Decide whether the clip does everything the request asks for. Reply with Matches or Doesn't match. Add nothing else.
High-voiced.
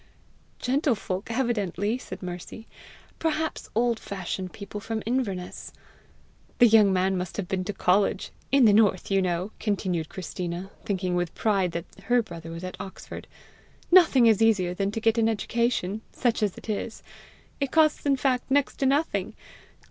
Matches